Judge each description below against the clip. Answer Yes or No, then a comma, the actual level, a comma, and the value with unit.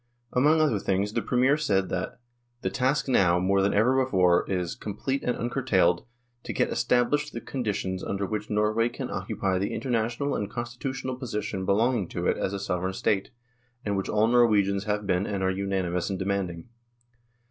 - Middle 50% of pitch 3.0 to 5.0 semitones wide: Yes, average, 4.1 semitones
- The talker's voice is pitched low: Yes, low, 105 Hz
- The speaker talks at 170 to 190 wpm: Yes, average, 180 wpm